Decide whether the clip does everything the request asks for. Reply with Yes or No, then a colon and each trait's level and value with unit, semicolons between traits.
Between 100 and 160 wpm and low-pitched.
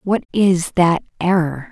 No: average, 140 wpm; medium, 180 Hz